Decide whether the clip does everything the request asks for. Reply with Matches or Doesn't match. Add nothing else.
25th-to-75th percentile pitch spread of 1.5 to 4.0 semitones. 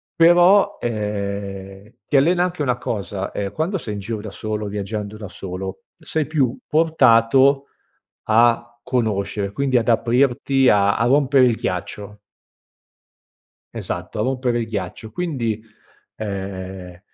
Doesn't match